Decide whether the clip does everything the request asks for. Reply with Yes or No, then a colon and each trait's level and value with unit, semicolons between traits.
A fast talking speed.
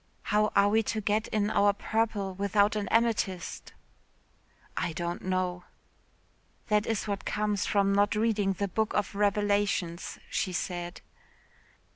No: slow, 135 wpm